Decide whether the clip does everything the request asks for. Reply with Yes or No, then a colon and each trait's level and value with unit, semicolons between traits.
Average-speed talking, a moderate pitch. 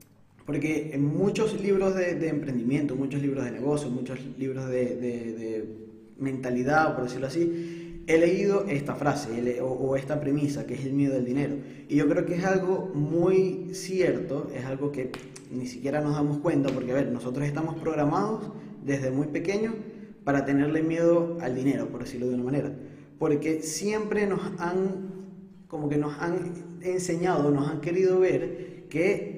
Yes: average, 170 wpm; medium, 150 Hz